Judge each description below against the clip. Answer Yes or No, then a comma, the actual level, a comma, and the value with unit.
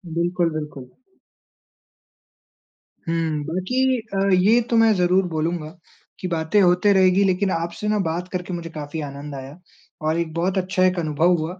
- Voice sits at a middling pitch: Yes, medium, 175 Hz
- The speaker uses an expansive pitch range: No, average, 2.8 semitones